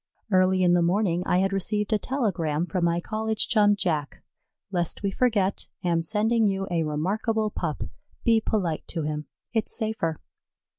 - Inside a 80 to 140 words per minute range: No, average, 160 wpm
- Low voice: No, high, 190 Hz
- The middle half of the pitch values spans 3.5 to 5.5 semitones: Yes, average, 4.1 semitones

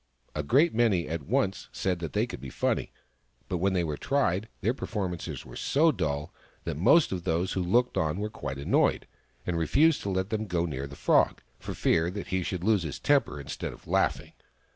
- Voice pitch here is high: No, very low, 90 Hz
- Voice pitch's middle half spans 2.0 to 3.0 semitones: No, average, 5.1 semitones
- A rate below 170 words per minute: No, fast, 205 wpm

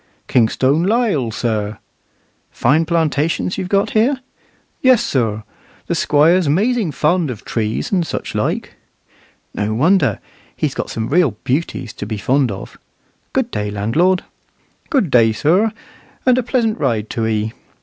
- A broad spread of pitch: Yes, wide, 9.0 semitones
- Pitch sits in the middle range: Yes, medium, 145 Hz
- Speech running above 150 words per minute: No, average, 140 wpm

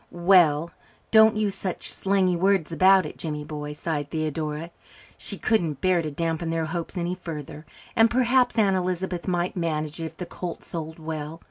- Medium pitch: Yes, medium, 170 Hz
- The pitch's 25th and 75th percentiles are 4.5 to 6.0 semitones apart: No, average, 3.2 semitones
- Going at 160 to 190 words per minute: Yes, average, 170 wpm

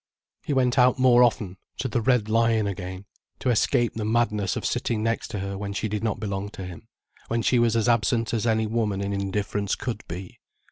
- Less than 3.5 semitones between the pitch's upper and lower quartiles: Yes, average, 2.8 semitones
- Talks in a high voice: No, low, 110 Hz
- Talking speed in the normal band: No, fast, 215 wpm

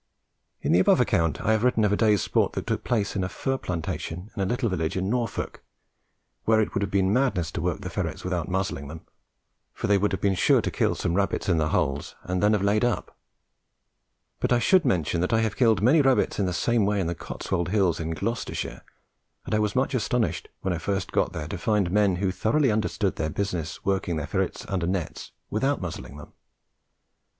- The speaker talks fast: Yes, fast, 220 wpm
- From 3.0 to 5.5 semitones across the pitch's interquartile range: Yes, average, 3.7 semitones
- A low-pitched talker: Yes, low, 100 Hz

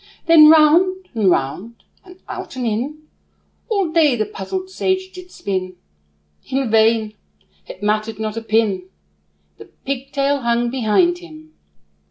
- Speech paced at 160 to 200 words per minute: No, slow, 135 wpm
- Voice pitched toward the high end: Yes, very high, 260 Hz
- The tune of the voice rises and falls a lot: Yes, wide, 7.3 semitones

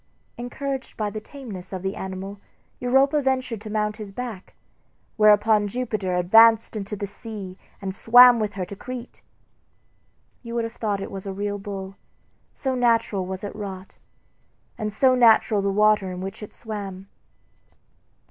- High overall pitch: Yes, high, 210 Hz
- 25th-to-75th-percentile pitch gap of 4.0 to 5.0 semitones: No, average, 3.1 semitones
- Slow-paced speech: No, average, 155 wpm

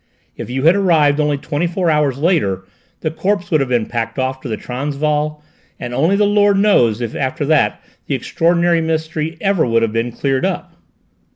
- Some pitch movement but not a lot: Yes, average, 4.6 semitones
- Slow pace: No, average, 190 wpm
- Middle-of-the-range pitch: Yes, medium, 150 Hz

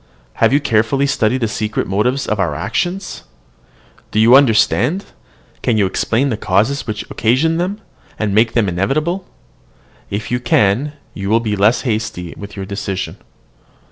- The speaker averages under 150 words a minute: No, average, 155 wpm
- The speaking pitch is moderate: No, low, 110 Hz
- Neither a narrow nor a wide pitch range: Yes, average, 5.0 semitones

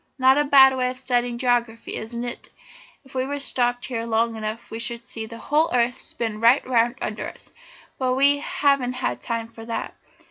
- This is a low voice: No, high, 245 Hz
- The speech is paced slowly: No, average, 185 wpm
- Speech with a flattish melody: Yes, narrow, 2.3 semitones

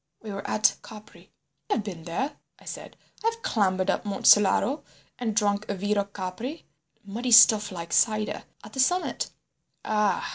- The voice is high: Yes, high, 210 Hz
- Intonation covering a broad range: No, average, 2.8 semitones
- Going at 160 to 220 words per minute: No, average, 150 wpm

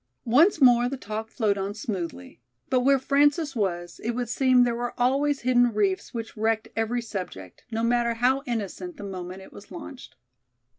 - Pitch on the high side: Yes, high, 235 Hz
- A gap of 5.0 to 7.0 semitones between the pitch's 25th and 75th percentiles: No, average, 3.9 semitones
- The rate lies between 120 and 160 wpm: No, average, 180 wpm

